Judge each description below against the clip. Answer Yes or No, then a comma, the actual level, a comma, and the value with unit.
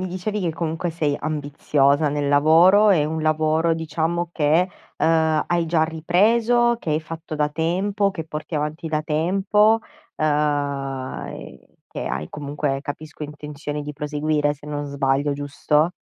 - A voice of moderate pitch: Yes, medium, 155 Hz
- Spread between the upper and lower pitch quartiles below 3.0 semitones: Yes, narrow, 2.4 semitones